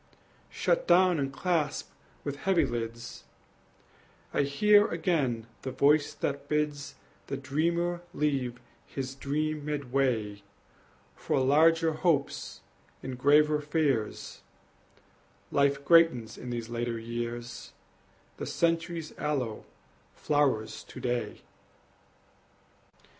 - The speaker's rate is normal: No, slow, 100 wpm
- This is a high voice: No, medium, 140 Hz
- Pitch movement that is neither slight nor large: Yes, average, 4.3 semitones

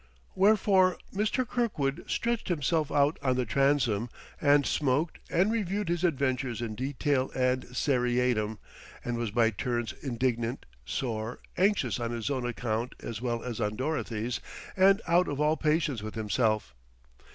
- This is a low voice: Yes, low, 130 Hz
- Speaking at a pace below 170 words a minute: Yes, average, 145 wpm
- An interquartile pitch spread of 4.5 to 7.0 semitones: Yes, average, 5.3 semitones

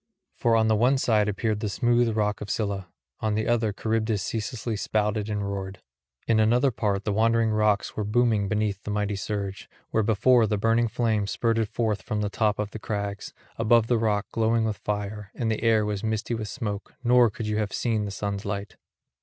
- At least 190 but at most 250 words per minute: Yes, average, 200 wpm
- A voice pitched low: Yes, low, 110 Hz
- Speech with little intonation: Yes, narrow, 1.6 semitones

